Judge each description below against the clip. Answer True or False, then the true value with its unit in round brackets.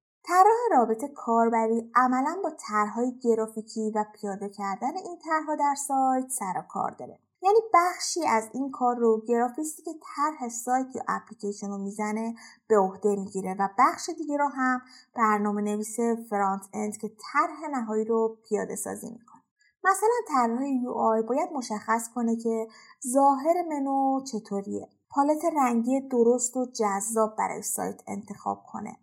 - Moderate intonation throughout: True (4.8 semitones)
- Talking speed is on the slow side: False (145 wpm)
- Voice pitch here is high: True (240 Hz)